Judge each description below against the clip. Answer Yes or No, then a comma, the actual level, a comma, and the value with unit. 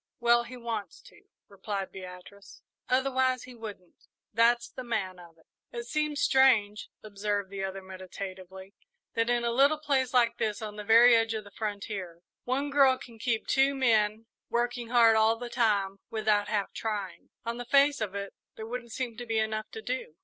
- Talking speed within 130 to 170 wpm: No, average, 185 wpm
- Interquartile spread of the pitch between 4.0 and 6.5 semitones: No, average, 3.3 semitones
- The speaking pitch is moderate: No, high, 225 Hz